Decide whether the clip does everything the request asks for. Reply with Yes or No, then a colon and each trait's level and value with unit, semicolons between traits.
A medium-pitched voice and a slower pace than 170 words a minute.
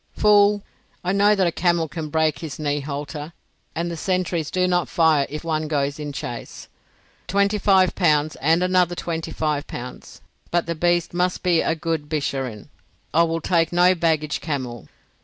No: medium, 165 Hz; average, 175 wpm